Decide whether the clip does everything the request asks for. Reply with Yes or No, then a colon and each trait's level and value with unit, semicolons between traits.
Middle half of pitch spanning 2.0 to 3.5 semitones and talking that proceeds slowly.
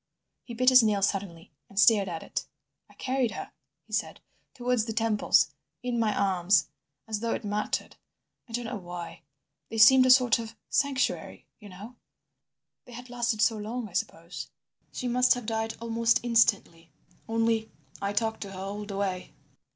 No: average, 3.1 semitones; average, 165 wpm